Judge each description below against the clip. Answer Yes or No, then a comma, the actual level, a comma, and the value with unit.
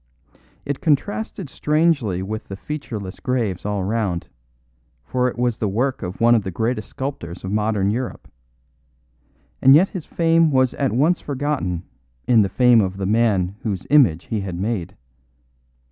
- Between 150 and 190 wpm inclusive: Yes, average, 160 wpm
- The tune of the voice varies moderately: No, wide, 6.0 semitones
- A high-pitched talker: No, low, 115 Hz